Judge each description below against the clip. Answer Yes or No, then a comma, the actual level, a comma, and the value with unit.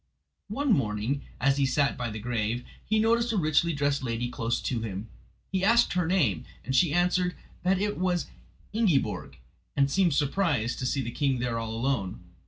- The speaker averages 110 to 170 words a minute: No, average, 185 wpm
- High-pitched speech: No, medium, 140 Hz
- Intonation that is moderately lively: No, wide, 7.3 semitones